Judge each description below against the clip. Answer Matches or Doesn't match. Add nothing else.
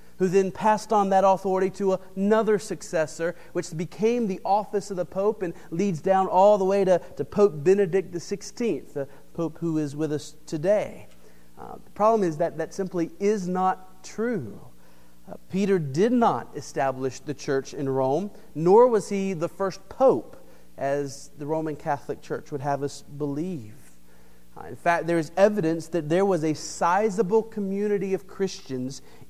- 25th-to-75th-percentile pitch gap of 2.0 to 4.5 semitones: Doesn't match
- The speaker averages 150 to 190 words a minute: Matches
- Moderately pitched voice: Matches